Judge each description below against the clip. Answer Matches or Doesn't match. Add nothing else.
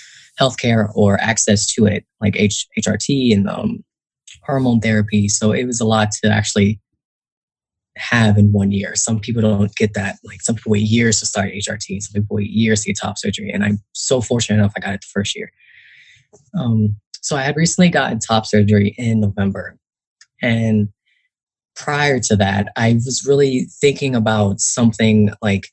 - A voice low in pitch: Matches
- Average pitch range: Doesn't match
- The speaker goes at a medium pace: Matches